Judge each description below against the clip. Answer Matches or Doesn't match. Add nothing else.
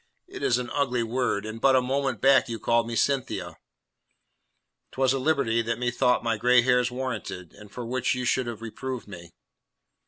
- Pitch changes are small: Matches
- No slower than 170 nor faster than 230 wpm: Matches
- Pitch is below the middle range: Matches